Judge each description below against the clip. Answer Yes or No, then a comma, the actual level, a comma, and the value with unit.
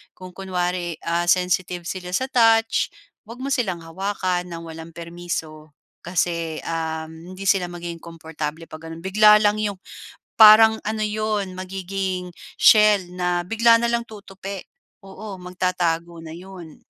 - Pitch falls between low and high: Yes, medium, 180 Hz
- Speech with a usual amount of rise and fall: Yes, average, 3.5 semitones